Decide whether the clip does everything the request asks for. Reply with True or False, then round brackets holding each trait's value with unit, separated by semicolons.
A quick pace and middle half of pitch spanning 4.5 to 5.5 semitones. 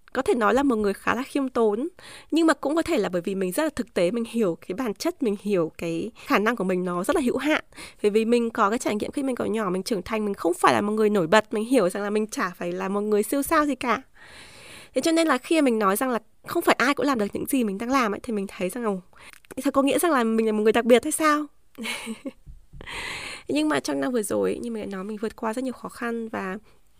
True (295 wpm; 5.1 semitones)